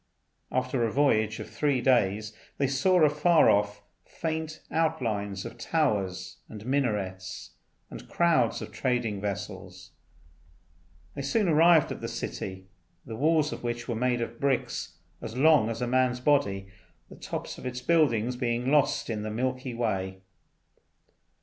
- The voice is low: Yes, low, 120 Hz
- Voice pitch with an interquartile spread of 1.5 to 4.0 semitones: No, average, 5.1 semitones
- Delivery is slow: No, average, 145 wpm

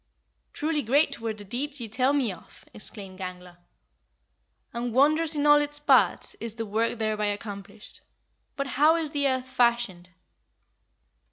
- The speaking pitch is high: Yes, high, 240 Hz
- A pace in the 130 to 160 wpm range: Yes, average, 150 wpm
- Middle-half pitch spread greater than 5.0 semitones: Yes, wide, 5.6 semitones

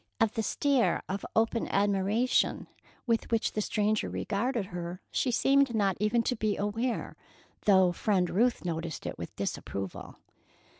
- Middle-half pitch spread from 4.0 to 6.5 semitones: No, average, 3.4 semitones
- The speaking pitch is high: Yes, high, 215 Hz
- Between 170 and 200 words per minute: No, average, 145 wpm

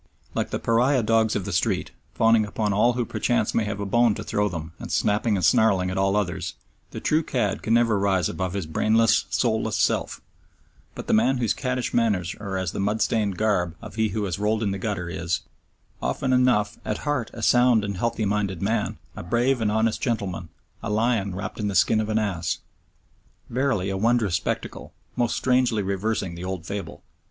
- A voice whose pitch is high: No, low, 105 Hz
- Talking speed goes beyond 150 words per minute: Yes, fast, 205 wpm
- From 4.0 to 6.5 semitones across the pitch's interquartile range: No, average, 3.0 semitones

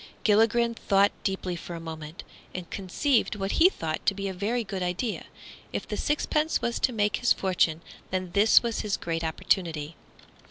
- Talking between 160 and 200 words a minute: Yes, average, 175 wpm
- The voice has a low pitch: No, high, 195 Hz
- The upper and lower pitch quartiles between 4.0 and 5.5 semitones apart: Yes, average, 4.6 semitones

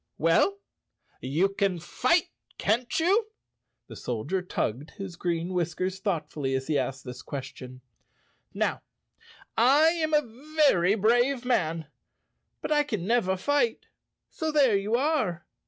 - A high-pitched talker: Yes, high, 195 Hz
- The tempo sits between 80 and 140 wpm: Yes, slow, 135 wpm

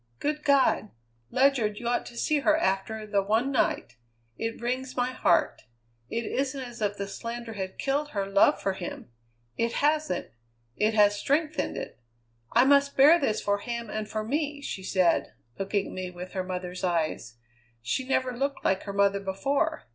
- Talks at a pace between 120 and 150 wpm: No, average, 180 wpm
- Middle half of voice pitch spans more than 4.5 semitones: Yes, wide, 5.6 semitones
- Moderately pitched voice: No, high, 225 Hz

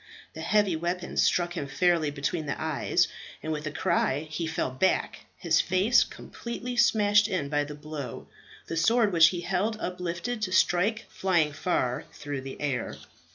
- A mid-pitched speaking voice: Yes, medium, 170 Hz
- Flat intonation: No, average, 4.2 semitones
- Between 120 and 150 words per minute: No, average, 165 wpm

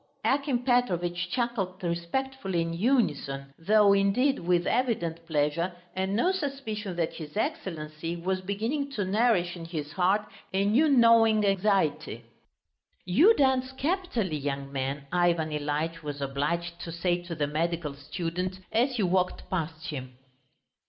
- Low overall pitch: No, medium, 180 Hz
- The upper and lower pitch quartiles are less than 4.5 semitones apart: No, wide, 5.5 semitones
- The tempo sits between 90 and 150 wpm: Yes, average, 140 wpm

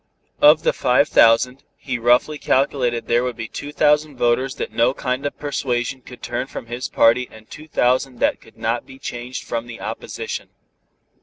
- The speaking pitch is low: Yes, low, 125 Hz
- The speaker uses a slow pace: No, average, 180 wpm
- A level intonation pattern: Yes, narrow, 2.3 semitones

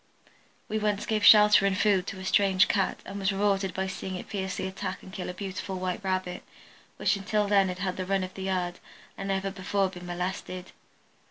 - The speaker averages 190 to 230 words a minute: Yes, fast, 205 wpm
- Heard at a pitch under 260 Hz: Yes, high, 190 Hz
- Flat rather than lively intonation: Yes, narrow, 1.3 semitones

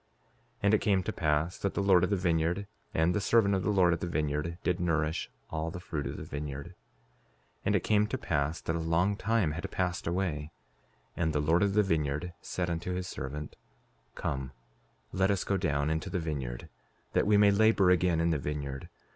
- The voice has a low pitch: Yes, very low, 85 Hz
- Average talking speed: No, fast, 215 wpm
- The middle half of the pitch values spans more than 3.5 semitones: Yes, average, 3.9 semitones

